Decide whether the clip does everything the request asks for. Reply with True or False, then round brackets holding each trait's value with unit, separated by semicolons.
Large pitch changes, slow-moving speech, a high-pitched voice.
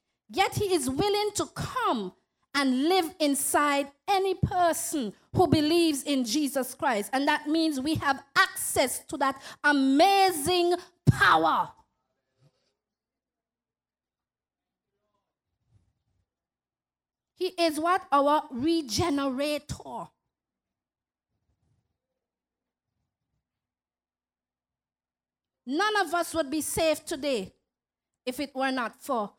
True (6.0 semitones; 90 wpm; 290 Hz)